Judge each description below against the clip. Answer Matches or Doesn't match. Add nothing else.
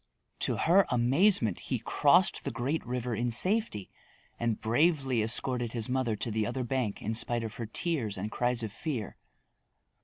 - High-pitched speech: Doesn't match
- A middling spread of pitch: Matches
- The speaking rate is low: Doesn't match